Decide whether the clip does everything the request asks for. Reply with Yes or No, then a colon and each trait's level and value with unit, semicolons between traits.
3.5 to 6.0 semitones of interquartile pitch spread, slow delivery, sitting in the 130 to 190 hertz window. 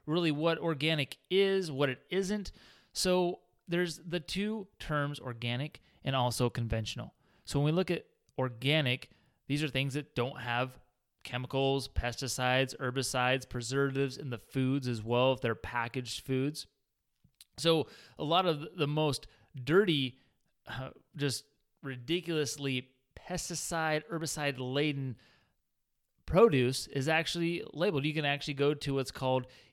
Yes: average, 3.8 semitones; slow, 130 wpm; medium, 140 Hz